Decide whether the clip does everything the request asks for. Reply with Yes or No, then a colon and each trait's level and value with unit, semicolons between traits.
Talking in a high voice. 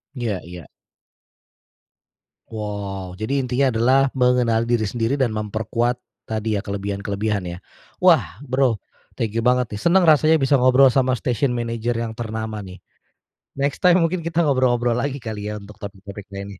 No: low, 115 Hz